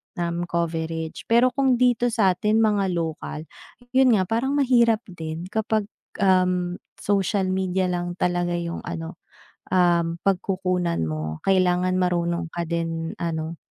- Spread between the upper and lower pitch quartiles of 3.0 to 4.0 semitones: Yes, average, 3.5 semitones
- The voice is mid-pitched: Yes, medium, 180 Hz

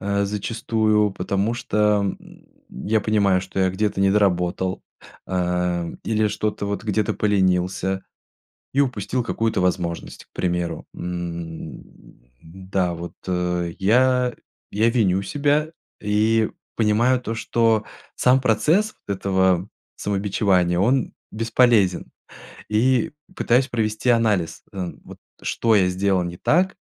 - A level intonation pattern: No, average, 3.6 semitones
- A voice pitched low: Yes, low, 100 Hz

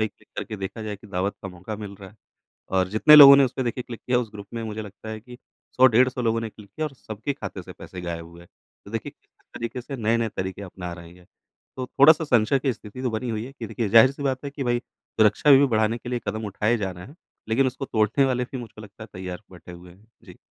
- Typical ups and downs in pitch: Yes, average, 4.0 semitones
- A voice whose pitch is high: No, low, 110 Hz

